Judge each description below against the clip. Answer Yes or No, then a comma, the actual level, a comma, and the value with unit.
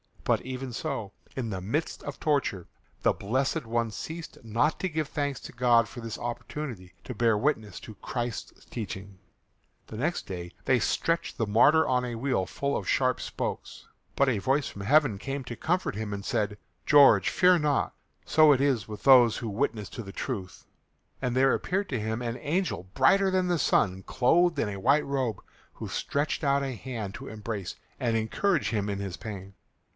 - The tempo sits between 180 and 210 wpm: Yes, average, 190 wpm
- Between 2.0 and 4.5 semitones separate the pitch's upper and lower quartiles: No, average, 5.1 semitones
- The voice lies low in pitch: Yes, low, 125 Hz